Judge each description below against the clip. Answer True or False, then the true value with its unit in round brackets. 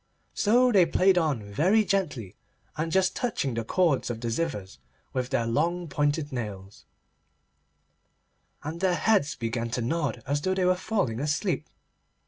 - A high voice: False (150 Hz)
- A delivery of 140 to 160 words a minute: True (150 wpm)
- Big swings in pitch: True (7.7 semitones)